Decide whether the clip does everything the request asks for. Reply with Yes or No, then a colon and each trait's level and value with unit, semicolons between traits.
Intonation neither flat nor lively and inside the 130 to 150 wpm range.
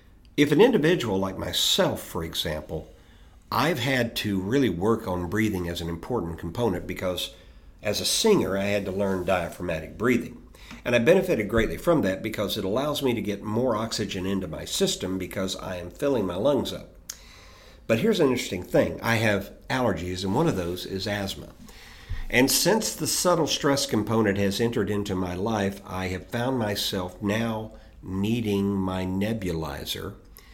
No: average, 3.9 semitones; average, 165 wpm